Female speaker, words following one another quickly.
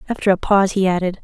Yes: female; fast, 240 wpm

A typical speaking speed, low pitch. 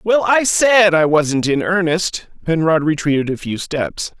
No: average, 170 wpm; medium, 170 Hz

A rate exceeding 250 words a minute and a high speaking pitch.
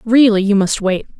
No: average, 200 wpm; high, 210 Hz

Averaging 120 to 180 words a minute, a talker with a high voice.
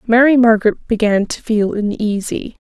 Yes: slow, 135 wpm; high, 220 Hz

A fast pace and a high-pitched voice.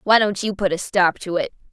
Yes: fast, 280 wpm; high, 200 Hz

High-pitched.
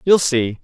No: medium, 140 Hz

